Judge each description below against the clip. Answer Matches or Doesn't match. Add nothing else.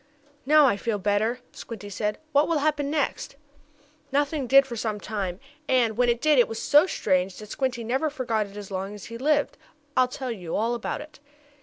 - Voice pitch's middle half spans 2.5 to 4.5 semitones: Doesn't match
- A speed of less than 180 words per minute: Doesn't match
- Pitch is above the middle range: Matches